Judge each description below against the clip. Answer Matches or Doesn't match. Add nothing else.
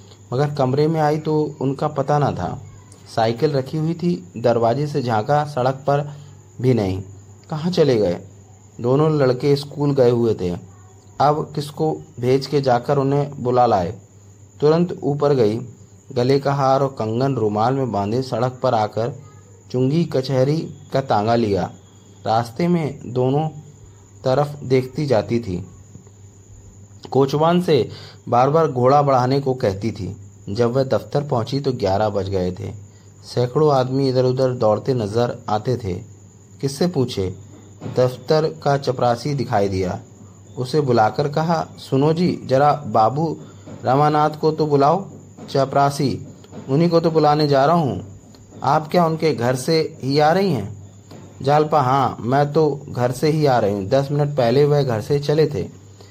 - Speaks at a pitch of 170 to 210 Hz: Doesn't match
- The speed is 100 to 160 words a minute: Matches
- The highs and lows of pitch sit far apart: Matches